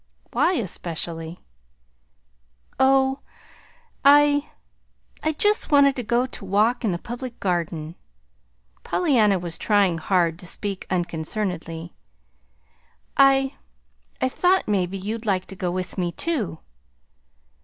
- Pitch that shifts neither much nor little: No, wide, 7.2 semitones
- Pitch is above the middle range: Yes, high, 205 Hz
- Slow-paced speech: Yes, slow, 110 wpm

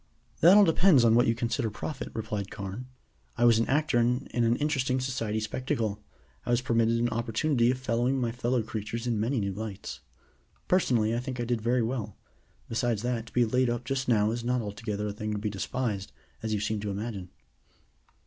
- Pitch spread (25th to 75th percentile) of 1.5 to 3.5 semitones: Yes, narrow, 2.6 semitones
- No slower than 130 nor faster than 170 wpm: No, average, 200 wpm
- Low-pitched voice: Yes, low, 115 Hz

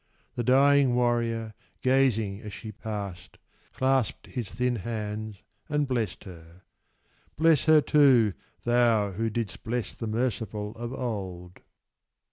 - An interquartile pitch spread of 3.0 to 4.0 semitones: Yes, average, 3.3 semitones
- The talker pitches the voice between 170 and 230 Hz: No, low, 115 Hz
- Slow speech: Yes, slow, 120 wpm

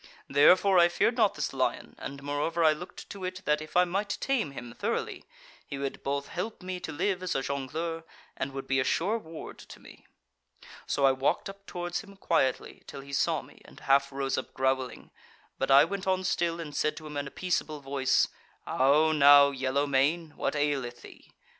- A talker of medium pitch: Yes, medium, 150 Hz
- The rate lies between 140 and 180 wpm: No, fast, 205 wpm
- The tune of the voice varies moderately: Yes, average, 4.4 semitones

